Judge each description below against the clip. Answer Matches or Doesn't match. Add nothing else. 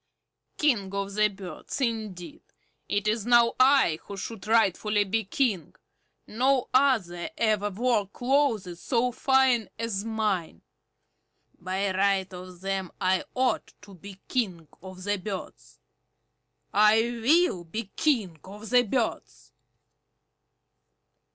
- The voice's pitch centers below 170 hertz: Doesn't match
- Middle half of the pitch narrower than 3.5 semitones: Doesn't match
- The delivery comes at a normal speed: Doesn't match